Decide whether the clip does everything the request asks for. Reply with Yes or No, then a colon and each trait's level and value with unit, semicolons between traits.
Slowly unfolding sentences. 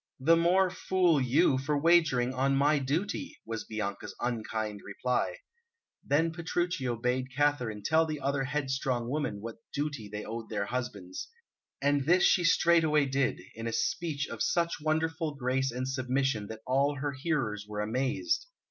No: average, 155 wpm